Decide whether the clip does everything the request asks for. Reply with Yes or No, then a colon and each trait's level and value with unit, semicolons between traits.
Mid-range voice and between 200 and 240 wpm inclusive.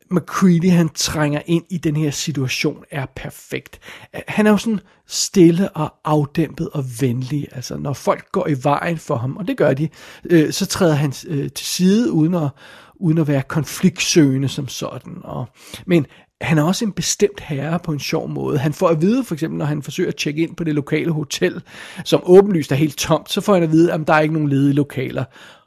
Yes: medium, 160 Hz; average, 215 wpm